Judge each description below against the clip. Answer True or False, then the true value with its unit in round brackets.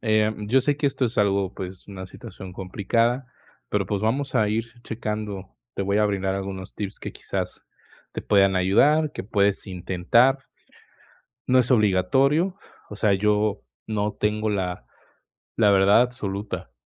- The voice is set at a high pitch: False (105 Hz)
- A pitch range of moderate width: True (3.2 semitones)